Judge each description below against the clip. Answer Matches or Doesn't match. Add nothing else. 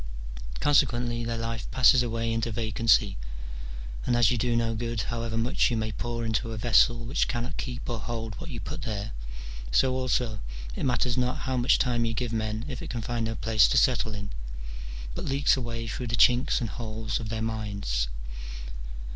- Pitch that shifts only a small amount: Matches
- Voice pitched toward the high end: Doesn't match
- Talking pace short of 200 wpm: Matches